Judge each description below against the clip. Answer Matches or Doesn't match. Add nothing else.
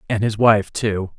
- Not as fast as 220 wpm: Matches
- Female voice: Doesn't match